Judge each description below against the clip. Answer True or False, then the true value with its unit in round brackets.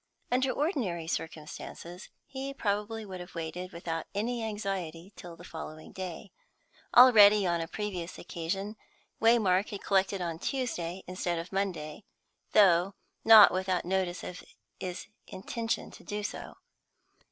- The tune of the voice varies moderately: True (3.5 semitones)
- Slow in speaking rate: True (130 wpm)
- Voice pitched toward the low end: False (190 Hz)